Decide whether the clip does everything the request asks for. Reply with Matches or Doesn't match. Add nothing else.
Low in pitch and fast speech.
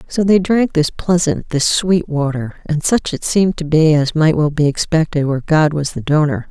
Doesn't match